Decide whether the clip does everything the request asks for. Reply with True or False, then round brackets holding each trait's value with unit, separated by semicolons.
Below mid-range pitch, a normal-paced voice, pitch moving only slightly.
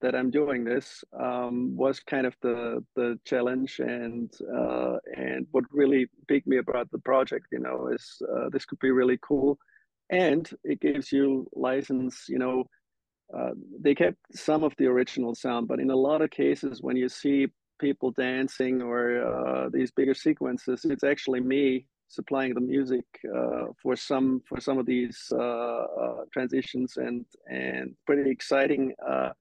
True (125 Hz; 165 wpm; 2.0 semitones)